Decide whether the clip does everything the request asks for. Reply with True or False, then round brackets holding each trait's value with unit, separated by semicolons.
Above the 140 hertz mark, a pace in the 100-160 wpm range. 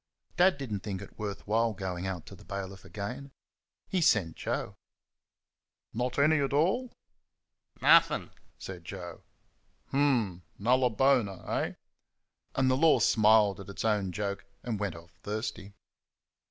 False (105 Hz; 140 wpm)